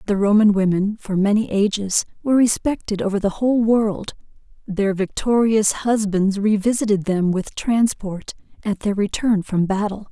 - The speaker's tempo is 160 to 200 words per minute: No, average, 150 wpm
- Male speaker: No, female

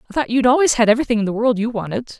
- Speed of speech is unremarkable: No, fast, 300 wpm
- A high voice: Yes, high, 235 Hz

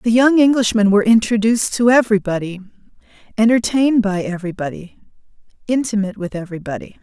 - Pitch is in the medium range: No, high, 215 Hz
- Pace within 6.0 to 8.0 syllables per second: Yes, 6.7 syllables/s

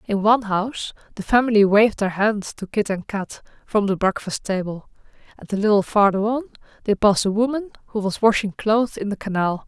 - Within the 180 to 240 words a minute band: Yes, average, 200 wpm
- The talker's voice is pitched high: Yes, high, 210 Hz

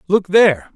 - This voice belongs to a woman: No, male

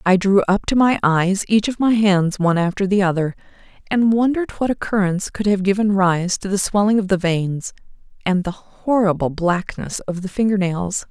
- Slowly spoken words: No, average, 190 wpm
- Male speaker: No, female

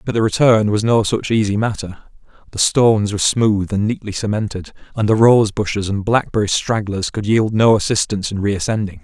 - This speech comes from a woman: No, male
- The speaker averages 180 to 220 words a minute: Yes, average, 200 wpm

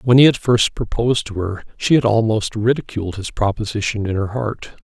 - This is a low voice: Yes, low, 110 Hz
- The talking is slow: No, average, 195 wpm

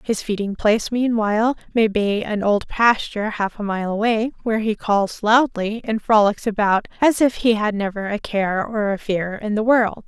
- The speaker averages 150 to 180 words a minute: No, average, 195 wpm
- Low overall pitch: No, high, 215 Hz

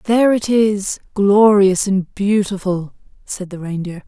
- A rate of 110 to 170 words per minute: Yes, slow, 135 wpm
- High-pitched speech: Yes, high, 200 Hz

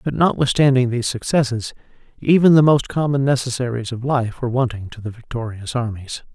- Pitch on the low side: Yes, low, 125 Hz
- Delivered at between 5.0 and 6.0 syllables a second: Yes, 5.8 syllables/s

